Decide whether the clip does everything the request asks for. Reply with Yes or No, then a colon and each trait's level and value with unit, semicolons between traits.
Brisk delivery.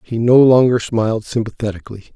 No: average, 140 wpm